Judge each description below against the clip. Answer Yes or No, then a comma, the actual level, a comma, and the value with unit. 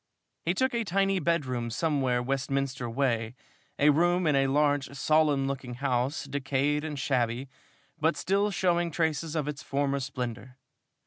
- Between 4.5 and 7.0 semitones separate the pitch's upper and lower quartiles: No, average, 3.5 semitones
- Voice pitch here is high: No, medium, 140 Hz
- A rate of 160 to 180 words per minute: No, average, 145 wpm